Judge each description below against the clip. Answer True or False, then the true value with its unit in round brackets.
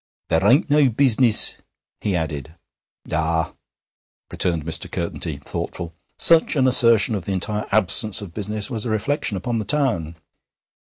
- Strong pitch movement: True (6.1 semitones)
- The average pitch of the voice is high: False (105 Hz)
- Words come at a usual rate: True (145 wpm)